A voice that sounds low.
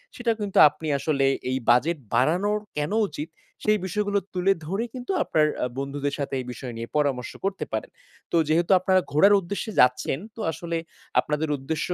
No: medium, 160 Hz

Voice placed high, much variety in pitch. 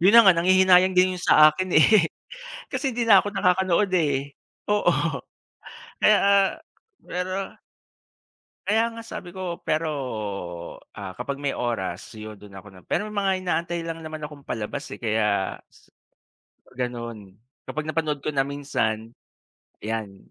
No: medium, 160 Hz; wide, 7.8 semitones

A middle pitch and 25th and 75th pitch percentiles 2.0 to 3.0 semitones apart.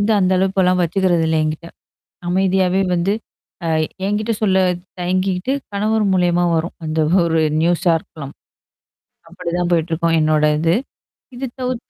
Yes: medium, 180 Hz; narrow, 2.4 semitones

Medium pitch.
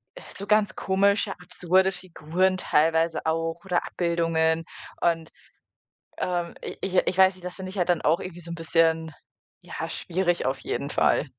Yes: medium, 175 Hz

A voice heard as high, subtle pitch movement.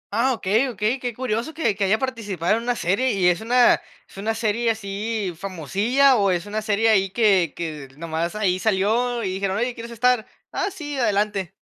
No: high, 215 Hz; average, 3.7 semitones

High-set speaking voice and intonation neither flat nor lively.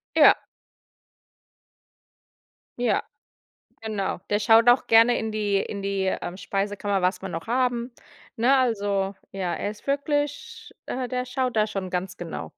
Yes: high, 215 Hz; average, 4.2 semitones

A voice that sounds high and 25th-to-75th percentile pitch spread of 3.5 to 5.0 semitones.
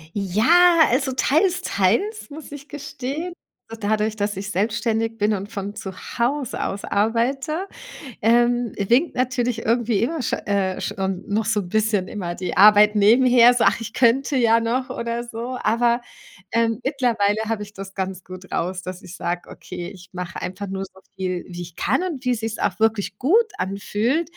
Yes: high, 225 Hz; average, 4.2 semitones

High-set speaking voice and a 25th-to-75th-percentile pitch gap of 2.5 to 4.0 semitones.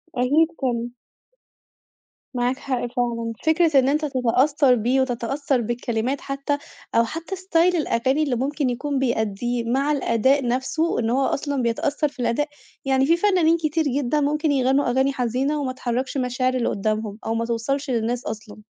Yes: very high, 260 Hz; average, 3.3 semitones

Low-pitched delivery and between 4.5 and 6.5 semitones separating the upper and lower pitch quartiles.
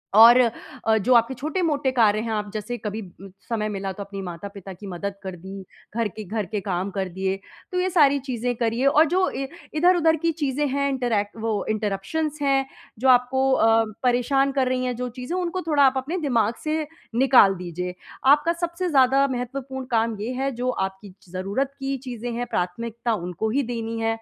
No: high, 245 Hz; average, 4.8 semitones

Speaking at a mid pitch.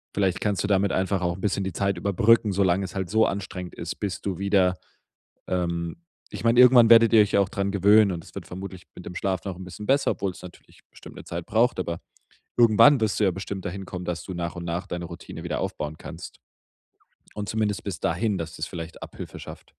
No: very low, 95 Hz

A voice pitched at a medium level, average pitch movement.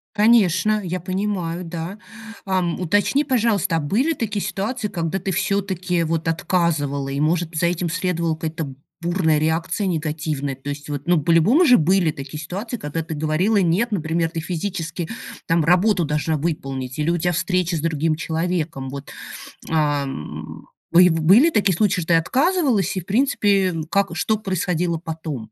Yes: medium, 170 Hz; average, 3.8 semitones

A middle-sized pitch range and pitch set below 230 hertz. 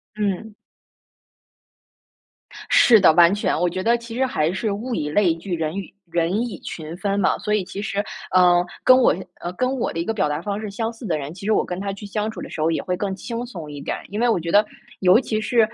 Yes: average, 4.2 semitones; high, 200 Hz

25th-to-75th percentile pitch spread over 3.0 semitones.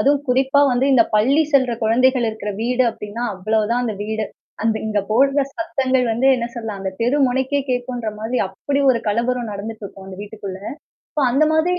Yes: average, 3.4 semitones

